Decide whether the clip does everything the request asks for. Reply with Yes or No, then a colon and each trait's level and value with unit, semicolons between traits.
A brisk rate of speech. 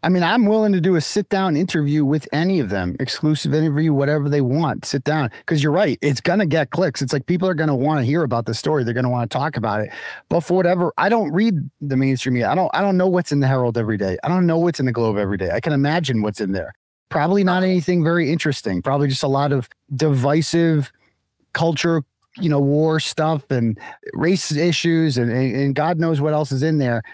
Yes: fast, 240 wpm